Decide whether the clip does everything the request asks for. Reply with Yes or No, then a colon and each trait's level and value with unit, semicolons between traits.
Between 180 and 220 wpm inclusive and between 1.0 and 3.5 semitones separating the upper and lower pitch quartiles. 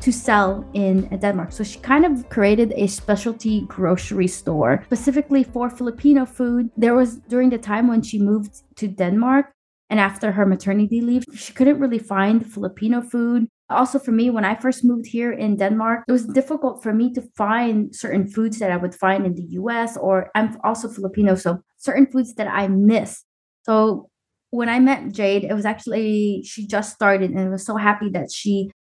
Yes: average, 190 wpm; average, 3.2 semitones